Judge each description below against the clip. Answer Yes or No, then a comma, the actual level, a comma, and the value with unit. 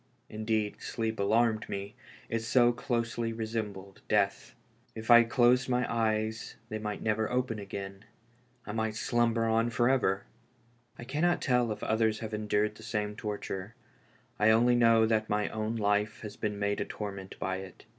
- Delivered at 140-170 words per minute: Yes, average, 165 wpm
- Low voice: Yes, low, 110 Hz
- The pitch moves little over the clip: Yes, narrow, 2.0 semitones